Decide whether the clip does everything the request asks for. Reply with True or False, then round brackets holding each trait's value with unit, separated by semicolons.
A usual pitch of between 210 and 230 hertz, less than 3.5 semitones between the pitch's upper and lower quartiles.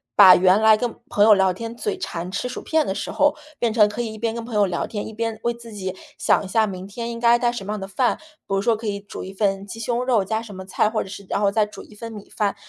True (215 Hz; 2.9 semitones)